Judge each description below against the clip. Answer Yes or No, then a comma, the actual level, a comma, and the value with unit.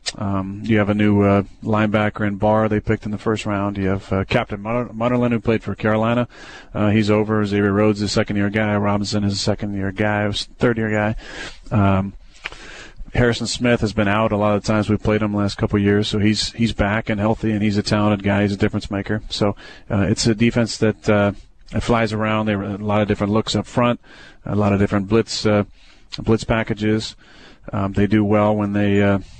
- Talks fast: Yes, fast, 220 wpm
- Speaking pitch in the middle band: No, low, 105 Hz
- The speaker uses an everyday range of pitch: No, narrow, 1.3 semitones